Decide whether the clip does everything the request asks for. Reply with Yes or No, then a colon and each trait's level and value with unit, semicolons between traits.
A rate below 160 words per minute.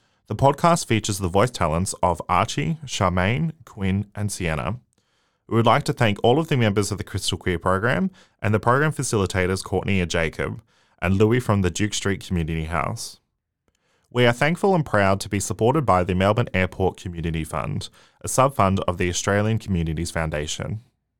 No: average, 180 wpm